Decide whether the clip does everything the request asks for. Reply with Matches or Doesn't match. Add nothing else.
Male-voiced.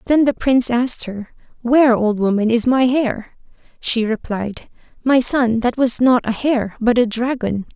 Doesn't match